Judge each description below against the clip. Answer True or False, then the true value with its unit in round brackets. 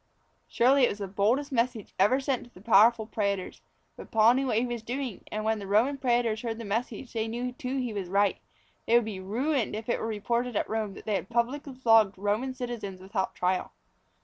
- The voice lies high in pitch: True (225 Hz)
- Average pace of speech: False (220 wpm)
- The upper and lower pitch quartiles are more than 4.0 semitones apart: False (3.3 semitones)